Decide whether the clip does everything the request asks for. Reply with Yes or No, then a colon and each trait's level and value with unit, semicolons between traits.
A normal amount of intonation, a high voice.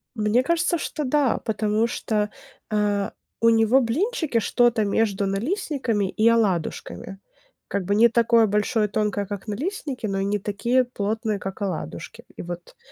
Yes: average, 3.2 semitones; high, 220 Hz